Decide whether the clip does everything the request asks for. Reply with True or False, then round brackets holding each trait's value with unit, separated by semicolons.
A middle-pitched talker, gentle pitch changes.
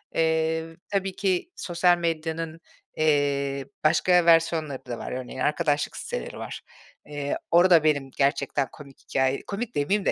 False (155 Hz; 3.3 semitones)